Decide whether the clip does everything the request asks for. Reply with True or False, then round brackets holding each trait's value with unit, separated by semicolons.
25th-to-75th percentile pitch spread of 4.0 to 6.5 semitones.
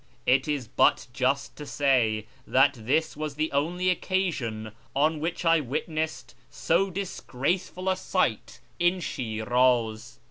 True (5.2 semitones)